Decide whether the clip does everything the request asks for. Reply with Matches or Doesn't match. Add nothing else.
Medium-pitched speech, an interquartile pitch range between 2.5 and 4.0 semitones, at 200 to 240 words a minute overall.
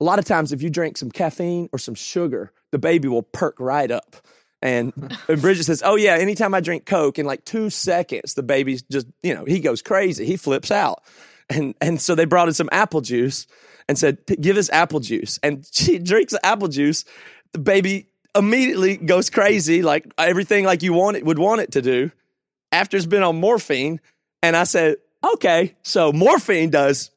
Doesn't match